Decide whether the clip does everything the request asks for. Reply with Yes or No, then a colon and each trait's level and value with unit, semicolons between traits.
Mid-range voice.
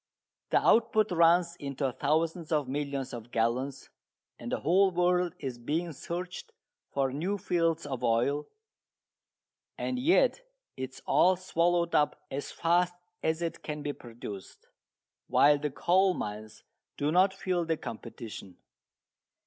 Yes: medium, 160 Hz